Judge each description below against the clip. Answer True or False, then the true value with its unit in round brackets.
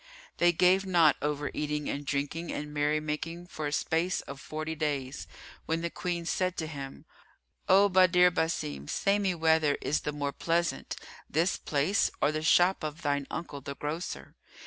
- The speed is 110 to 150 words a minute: False (170 wpm)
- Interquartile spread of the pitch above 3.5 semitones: False (2.9 semitones)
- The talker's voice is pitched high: False (155 Hz)